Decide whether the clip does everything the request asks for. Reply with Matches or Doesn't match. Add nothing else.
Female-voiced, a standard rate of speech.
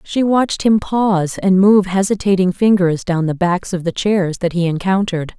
Matches